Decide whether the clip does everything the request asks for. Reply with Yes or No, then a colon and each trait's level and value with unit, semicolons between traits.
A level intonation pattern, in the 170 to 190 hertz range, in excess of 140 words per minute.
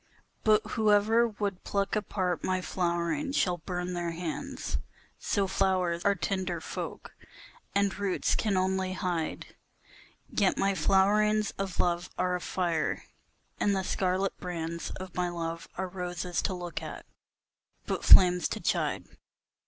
No: narrow, 2.1 semitones; medium, 185 Hz; slow, 135 wpm